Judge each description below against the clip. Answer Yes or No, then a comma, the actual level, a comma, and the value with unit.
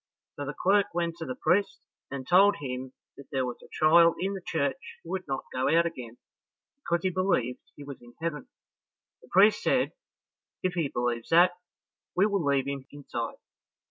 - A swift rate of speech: No, average, 185 wpm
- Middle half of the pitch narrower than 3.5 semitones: No, average, 5.3 semitones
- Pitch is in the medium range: Yes, medium, 160 Hz